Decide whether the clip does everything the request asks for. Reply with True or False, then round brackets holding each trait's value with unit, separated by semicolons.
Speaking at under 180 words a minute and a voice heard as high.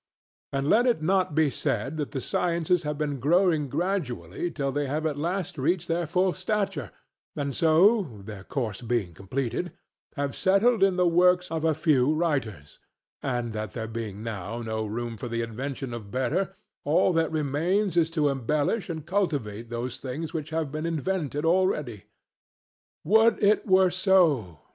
False (165 wpm; 150 Hz)